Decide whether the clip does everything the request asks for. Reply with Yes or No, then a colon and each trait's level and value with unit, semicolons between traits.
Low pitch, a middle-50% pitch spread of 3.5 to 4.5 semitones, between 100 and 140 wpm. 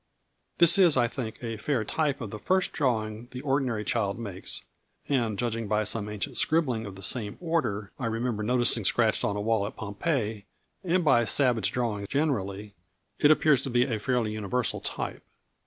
No: low, 115 Hz; average, 4.0 semitones; average, 180 wpm